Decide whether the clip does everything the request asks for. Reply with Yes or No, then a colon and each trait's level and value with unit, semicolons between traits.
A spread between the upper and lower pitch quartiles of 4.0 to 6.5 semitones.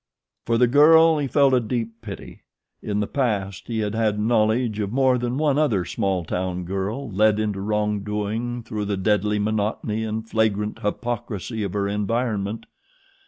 No: average, 2.7 semitones